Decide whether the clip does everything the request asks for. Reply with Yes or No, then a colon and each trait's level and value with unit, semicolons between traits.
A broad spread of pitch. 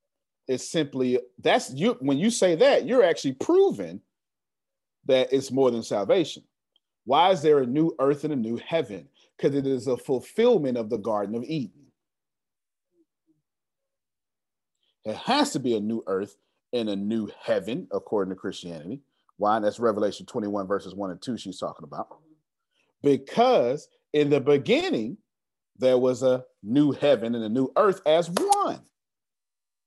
Yes: wide, 7.7 semitones